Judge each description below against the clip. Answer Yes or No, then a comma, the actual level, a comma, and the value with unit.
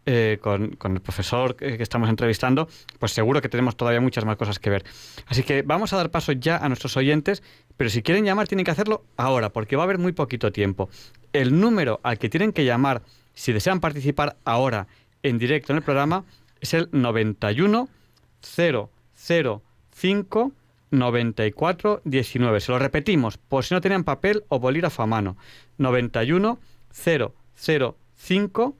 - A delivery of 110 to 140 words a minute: No, average, 165 wpm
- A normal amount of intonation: No, wide, 6.3 semitones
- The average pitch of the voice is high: No, low, 135 Hz